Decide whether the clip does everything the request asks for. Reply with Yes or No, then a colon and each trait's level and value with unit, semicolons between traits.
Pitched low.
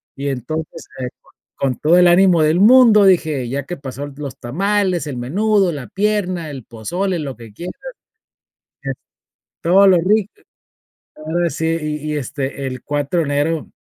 No: medium, 160 Hz